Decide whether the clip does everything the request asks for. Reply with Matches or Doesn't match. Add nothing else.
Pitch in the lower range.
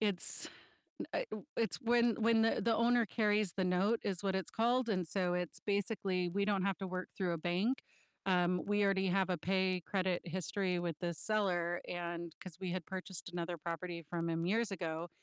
Doesn't match